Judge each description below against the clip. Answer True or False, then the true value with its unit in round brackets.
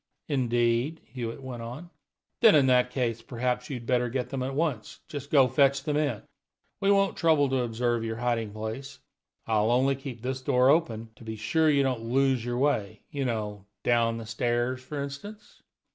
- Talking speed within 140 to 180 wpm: False (190 wpm)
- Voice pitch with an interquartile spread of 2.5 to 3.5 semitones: True (3.2 semitones)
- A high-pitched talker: False (125 Hz)